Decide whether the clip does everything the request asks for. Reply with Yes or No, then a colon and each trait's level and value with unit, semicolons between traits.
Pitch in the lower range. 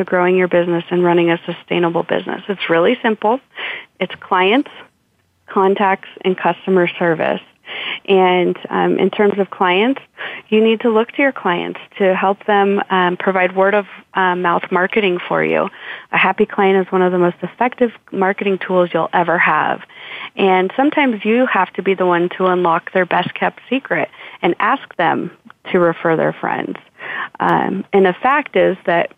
No: high, 190 Hz